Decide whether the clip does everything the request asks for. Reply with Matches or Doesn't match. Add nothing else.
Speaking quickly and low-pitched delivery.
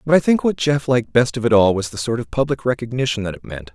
Matches